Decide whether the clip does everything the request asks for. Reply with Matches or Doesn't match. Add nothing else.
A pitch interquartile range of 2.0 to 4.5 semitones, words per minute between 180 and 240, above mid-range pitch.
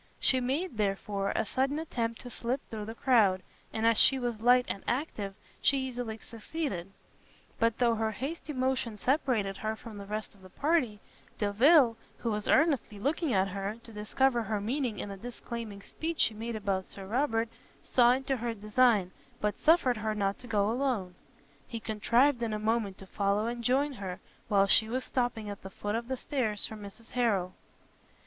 Matches